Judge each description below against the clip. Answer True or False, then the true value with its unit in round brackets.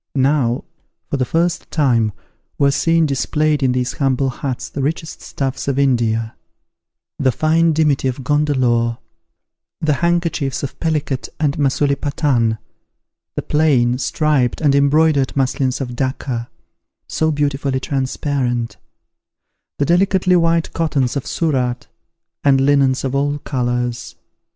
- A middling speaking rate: False (120 wpm)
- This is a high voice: False (140 Hz)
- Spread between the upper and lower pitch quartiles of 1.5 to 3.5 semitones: True (3.0 semitones)